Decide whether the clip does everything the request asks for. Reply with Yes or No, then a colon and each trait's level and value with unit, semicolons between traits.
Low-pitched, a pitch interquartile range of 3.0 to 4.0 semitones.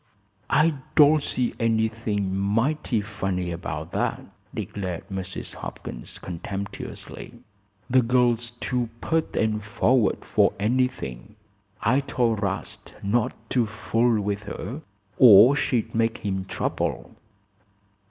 Yes: low, 110 Hz; average, 3.6 semitones